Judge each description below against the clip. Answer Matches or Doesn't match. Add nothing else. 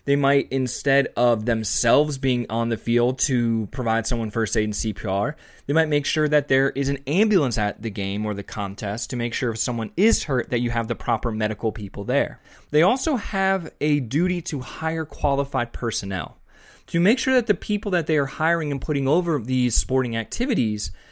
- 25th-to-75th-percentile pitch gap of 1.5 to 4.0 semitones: Doesn't match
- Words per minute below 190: Doesn't match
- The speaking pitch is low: Matches